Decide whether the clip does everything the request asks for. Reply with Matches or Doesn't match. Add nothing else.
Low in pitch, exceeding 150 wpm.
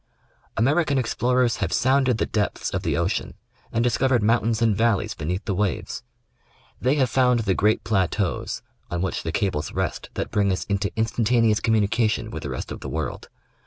Matches